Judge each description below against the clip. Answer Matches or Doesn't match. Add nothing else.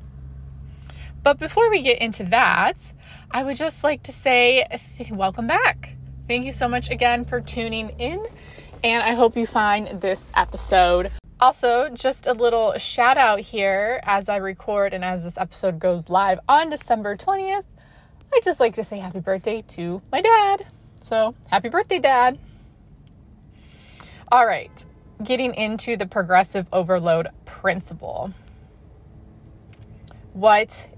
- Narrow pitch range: Doesn't match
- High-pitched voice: Matches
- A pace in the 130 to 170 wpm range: Matches